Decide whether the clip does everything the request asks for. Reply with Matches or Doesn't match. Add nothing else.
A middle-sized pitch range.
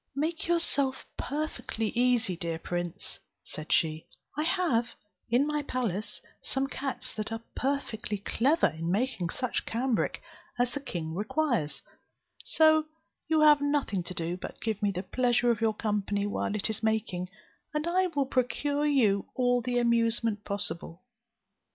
Doesn't match